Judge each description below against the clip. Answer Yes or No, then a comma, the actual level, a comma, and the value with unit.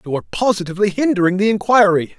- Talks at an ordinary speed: Yes, average, 165 wpm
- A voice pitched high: Yes, high, 195 Hz